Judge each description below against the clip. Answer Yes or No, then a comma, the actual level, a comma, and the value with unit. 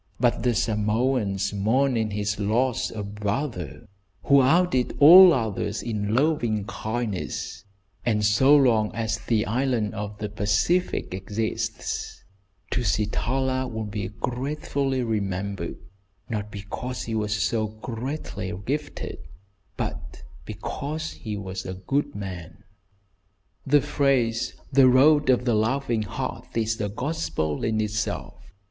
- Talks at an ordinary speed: No, slow, 120 wpm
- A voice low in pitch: Yes, low, 110 Hz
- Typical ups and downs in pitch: Yes, average, 4.0 semitones